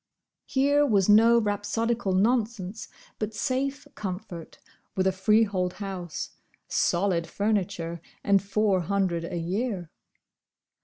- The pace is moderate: No, slow, 105 wpm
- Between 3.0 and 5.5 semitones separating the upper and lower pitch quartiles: Yes, average, 3.4 semitones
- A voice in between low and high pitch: No, high, 200 Hz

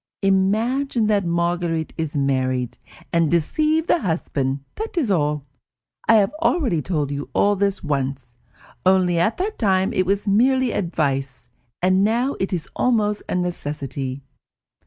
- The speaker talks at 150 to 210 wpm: No, average, 140 wpm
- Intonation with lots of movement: Yes, wide, 6.3 semitones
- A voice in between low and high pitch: Yes, medium, 180 Hz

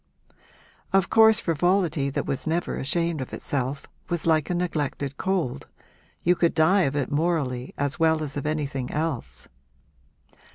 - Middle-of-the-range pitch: Yes, medium, 155 Hz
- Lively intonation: No, average, 3.8 semitones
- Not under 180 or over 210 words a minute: No, average, 150 wpm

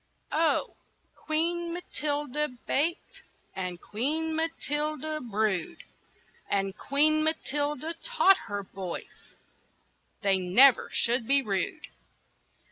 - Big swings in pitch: Yes, wide, 7.0 semitones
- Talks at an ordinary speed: No, slow, 90 wpm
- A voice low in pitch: No, very high, 290 Hz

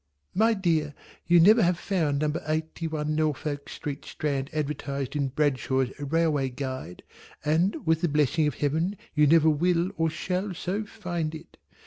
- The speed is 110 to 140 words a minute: No, average, 155 wpm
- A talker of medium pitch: Yes, medium, 155 Hz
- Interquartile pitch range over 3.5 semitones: No, average, 2.9 semitones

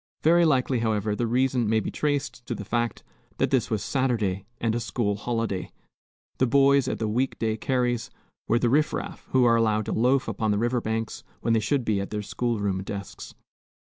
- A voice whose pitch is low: Yes, low, 115 Hz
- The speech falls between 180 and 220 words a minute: Yes, fast, 205 wpm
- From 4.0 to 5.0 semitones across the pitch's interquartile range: No, average, 3.1 semitones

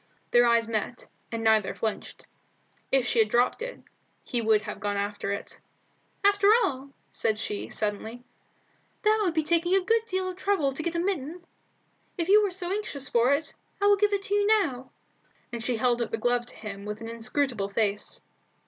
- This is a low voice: No, very high, 255 Hz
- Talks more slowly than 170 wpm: No, average, 195 wpm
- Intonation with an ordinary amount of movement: No, wide, 8.9 semitones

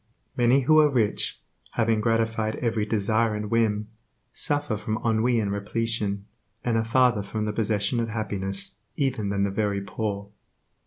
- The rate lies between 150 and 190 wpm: Yes, average, 155 wpm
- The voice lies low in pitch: Yes, low, 110 Hz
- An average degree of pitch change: No, narrow, 2.1 semitones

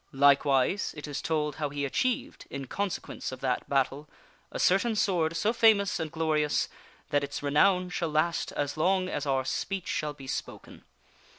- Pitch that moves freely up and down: No, average, 4.6 semitones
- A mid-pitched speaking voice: Yes, medium, 155 Hz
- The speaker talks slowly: No, average, 170 wpm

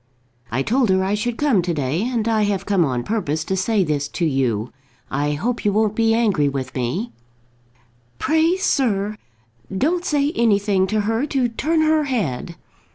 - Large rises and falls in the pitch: Yes, wide, 7.1 semitones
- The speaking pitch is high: Yes, high, 205 Hz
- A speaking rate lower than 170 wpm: No, average, 175 wpm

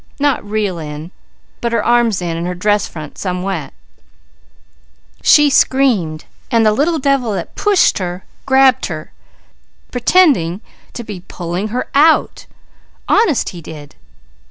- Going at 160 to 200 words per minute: No, slow, 135 wpm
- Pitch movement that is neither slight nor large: No, wide, 7.1 semitones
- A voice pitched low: No, high, 210 Hz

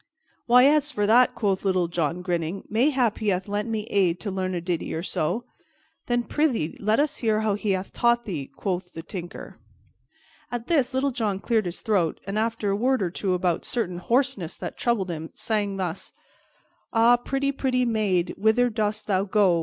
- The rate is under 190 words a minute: No, average, 195 wpm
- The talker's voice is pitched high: Yes, high, 210 Hz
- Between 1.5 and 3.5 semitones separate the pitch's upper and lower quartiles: No, average, 4.7 semitones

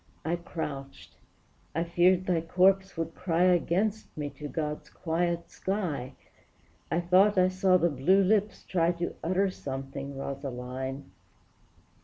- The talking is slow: Yes, slow, 130 wpm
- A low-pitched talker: No, medium, 170 Hz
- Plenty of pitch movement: No, average, 4.3 semitones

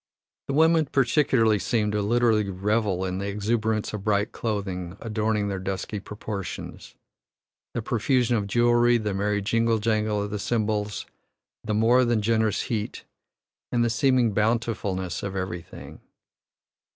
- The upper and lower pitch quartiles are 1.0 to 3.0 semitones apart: Yes, narrow, 2.5 semitones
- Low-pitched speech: Yes, low, 110 Hz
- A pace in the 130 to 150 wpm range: Yes, average, 140 wpm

